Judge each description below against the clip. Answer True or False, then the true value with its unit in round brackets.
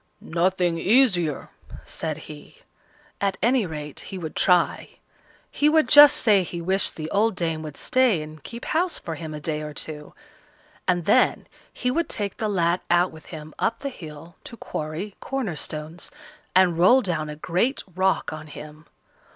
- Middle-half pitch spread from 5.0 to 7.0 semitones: True (5.4 semitones)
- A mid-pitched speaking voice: True (175 Hz)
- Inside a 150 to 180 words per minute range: True (170 wpm)